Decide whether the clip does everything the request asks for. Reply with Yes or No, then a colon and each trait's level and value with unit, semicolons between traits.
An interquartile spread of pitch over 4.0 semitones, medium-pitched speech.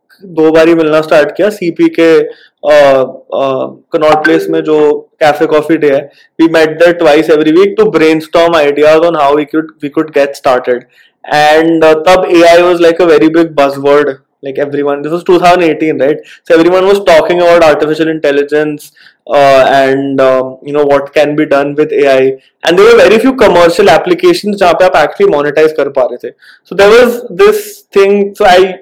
No: average, 3.7 semitones; medium, 155 Hz